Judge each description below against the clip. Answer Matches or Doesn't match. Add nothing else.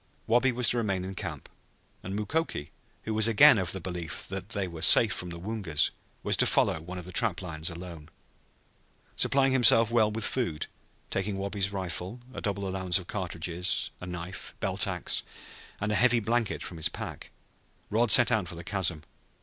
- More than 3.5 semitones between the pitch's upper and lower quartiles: Matches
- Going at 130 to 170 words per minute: Doesn't match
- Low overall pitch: Matches